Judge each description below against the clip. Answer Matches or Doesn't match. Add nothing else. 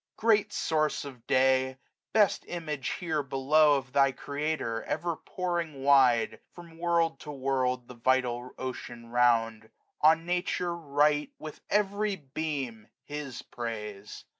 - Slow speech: Matches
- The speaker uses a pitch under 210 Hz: Matches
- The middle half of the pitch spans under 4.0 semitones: Doesn't match